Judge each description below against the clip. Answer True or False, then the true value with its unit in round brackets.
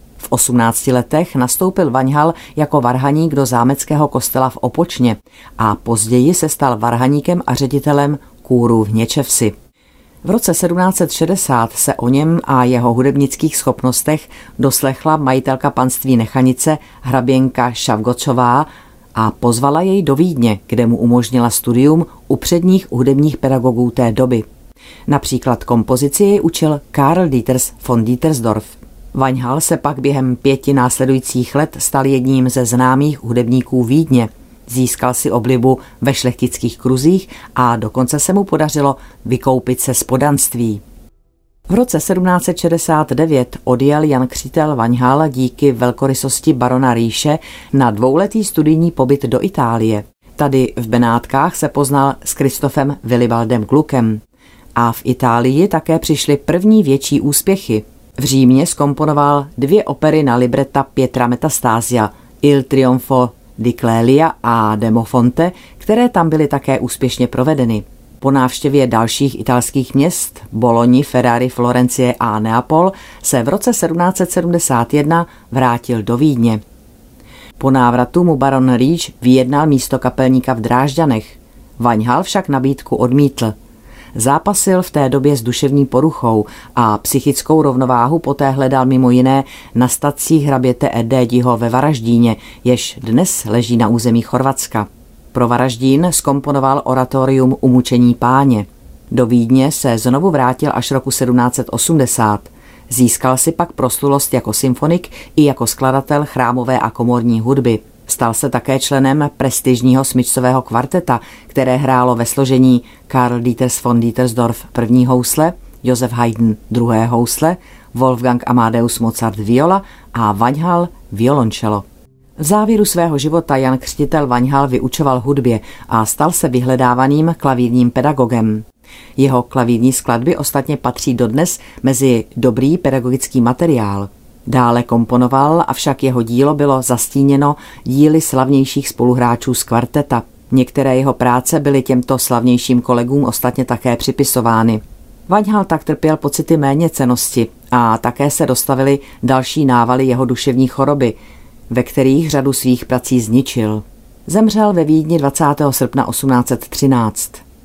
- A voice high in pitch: False (130 Hz)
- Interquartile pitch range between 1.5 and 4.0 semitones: True (2.9 semitones)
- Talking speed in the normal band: True (125 wpm)